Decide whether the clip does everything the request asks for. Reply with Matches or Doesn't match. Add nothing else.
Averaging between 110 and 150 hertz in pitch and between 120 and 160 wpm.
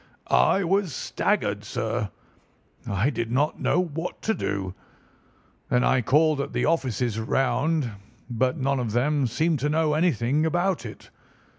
Matches